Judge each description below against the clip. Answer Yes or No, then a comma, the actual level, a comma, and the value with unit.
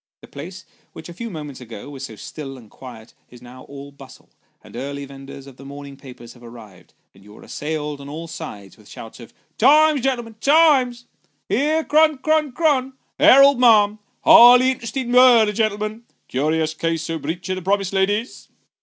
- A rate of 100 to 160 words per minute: No, average, 190 wpm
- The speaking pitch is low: No, medium, 165 Hz